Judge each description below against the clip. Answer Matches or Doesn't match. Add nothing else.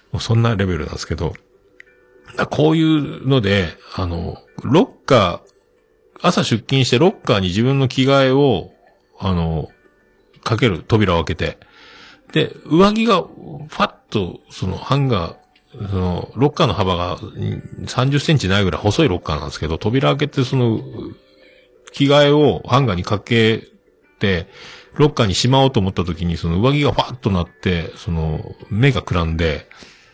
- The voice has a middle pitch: Doesn't match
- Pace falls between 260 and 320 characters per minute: Matches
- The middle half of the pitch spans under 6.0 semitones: Doesn't match